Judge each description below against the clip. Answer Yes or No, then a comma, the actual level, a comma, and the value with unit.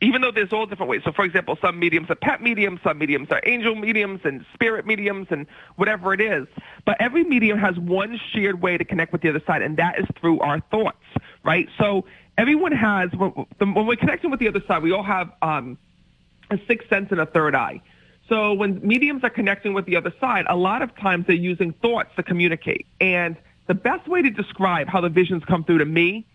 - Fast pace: Yes, fast, 225 wpm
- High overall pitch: Yes, high, 195 Hz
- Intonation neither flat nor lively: Yes, average, 3.9 semitones